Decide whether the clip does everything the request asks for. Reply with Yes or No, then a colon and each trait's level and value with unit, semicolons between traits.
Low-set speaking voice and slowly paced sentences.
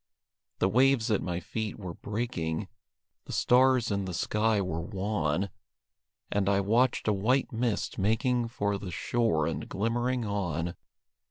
No: low, 105 Hz; average, 145 wpm